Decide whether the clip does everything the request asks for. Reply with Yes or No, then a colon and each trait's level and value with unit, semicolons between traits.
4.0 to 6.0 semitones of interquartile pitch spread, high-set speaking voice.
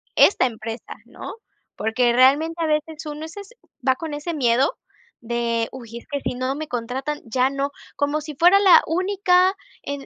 Yes: average, 4.6 semitones; very high, 285 Hz